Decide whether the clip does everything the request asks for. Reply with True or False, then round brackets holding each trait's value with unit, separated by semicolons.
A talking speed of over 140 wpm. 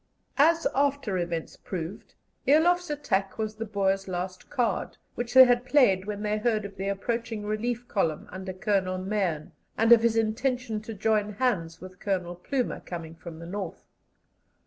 True (165 wpm)